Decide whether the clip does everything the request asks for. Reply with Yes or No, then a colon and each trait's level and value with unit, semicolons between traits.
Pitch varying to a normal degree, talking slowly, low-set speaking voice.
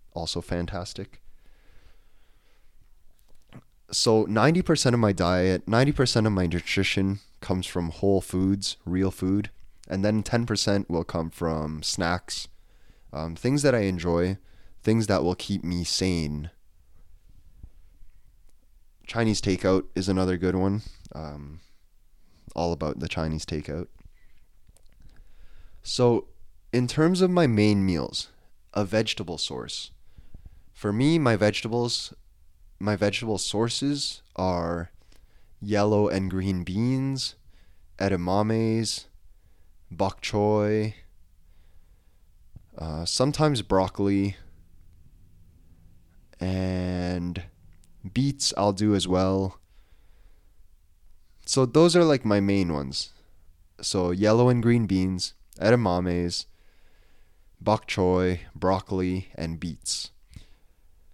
Yes: average, 3.7 semitones; slow, 95 wpm; very low, 90 Hz